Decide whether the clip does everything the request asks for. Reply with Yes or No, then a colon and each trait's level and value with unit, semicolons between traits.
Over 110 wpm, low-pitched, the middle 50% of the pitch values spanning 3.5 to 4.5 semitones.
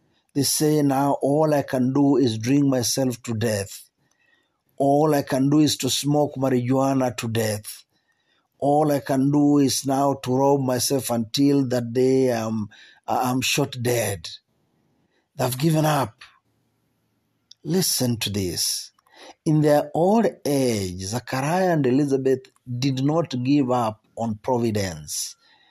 No: average, 135 wpm; low, 130 Hz; average, 2.8 semitones